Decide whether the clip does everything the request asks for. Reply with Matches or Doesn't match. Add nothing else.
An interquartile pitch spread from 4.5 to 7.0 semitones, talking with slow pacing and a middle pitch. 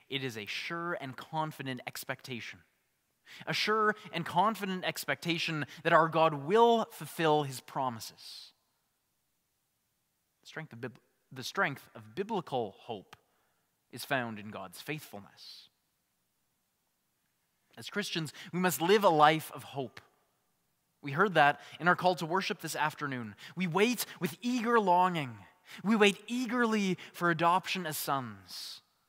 Matches